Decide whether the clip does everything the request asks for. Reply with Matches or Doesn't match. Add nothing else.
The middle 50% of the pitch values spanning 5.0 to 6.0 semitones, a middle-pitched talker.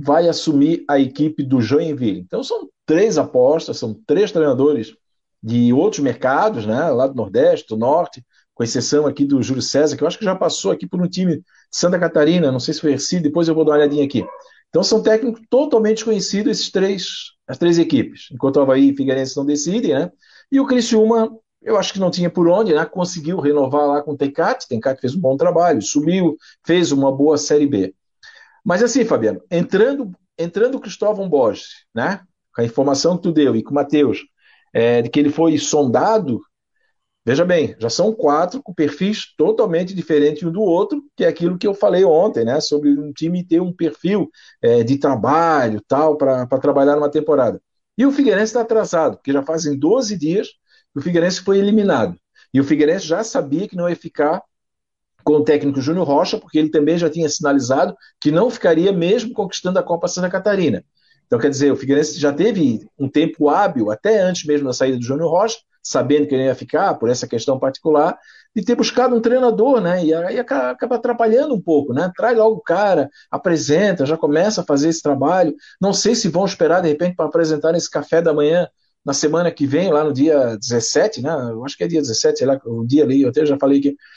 Matches